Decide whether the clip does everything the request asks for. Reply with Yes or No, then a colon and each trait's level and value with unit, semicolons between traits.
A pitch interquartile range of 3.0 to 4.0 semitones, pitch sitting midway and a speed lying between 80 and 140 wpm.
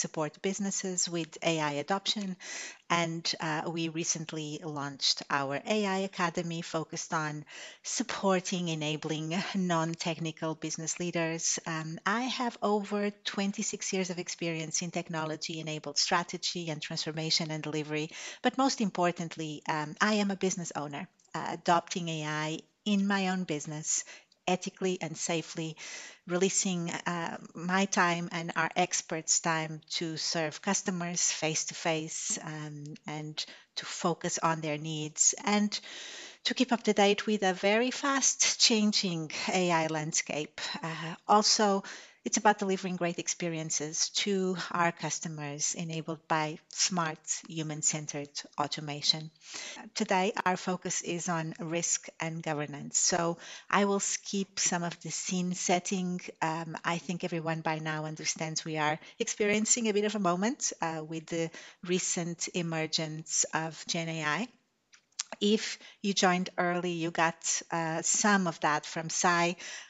Yes: average, 3.6 semitones; medium, 170 Hz; slow, 135 wpm